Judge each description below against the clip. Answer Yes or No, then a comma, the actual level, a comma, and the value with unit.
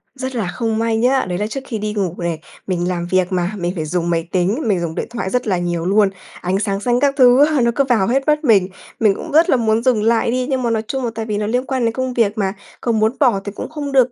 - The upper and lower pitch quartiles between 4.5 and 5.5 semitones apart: Yes, average, 5.0 semitones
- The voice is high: Yes, high, 225 Hz